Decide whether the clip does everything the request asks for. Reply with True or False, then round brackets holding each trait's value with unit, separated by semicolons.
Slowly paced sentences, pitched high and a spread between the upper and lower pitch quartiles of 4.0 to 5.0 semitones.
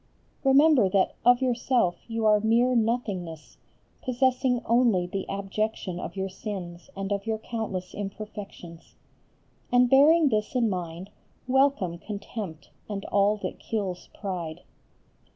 True (125 wpm; 210 Hz; 4.5 semitones)